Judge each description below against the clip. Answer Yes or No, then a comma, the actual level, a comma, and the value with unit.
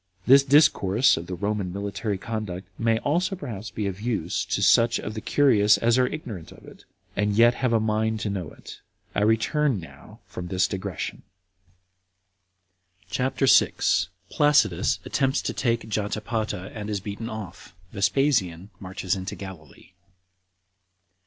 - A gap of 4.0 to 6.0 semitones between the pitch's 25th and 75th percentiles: No, average, 3.6 semitones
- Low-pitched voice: Yes, low, 105 Hz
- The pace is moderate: Yes, average, 145 wpm